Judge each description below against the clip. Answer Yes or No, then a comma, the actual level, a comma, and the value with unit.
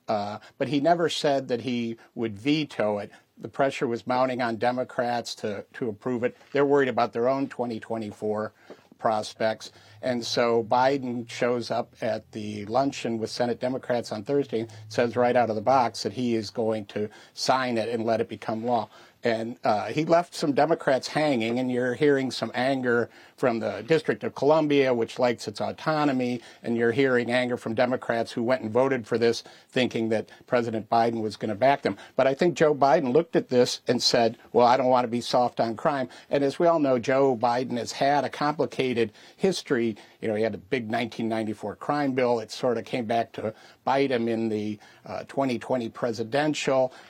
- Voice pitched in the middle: No, low, 120 Hz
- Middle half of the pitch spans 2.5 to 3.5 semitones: Yes, average, 2.8 semitones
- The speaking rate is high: No, average, 195 wpm